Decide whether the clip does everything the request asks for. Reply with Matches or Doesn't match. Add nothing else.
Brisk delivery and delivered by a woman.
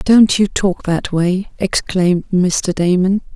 Doesn't match